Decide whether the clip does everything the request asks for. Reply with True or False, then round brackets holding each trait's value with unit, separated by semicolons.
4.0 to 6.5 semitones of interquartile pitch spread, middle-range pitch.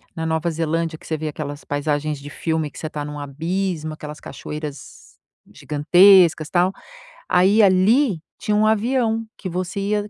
True (4.4 semitones; 165 Hz)